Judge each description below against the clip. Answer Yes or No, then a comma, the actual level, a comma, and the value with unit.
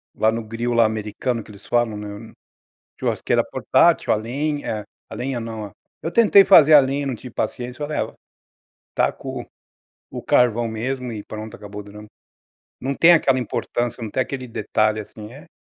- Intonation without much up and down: No, average, 3.6 semitones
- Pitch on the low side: Yes, low, 115 Hz